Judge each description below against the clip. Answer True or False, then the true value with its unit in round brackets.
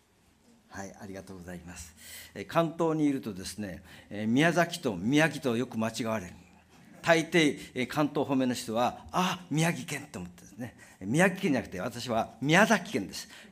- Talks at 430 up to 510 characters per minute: False (255 characters per minute)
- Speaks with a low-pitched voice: True (120 Hz)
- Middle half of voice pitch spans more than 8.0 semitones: True (8.4 semitones)